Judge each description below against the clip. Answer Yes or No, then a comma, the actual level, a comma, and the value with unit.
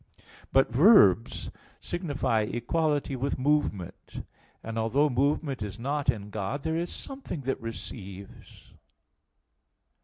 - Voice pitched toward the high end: No, low, 135 Hz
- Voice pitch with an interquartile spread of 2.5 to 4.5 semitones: No, average, 5.0 semitones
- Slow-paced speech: Yes, slow, 110 wpm